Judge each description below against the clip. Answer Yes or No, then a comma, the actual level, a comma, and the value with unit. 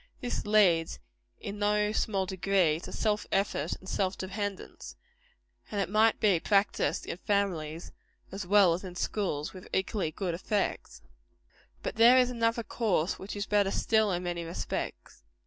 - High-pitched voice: Yes, high, 195 Hz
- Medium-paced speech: Yes, average, 150 wpm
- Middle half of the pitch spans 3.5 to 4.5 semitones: No, average, 2.9 semitones